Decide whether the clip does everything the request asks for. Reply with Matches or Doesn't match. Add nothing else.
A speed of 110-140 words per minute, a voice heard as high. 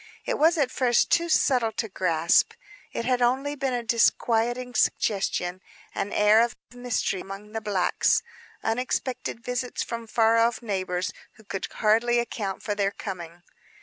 Doesn't match